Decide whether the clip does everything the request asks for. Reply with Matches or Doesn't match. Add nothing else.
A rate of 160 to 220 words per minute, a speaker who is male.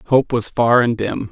Doesn't match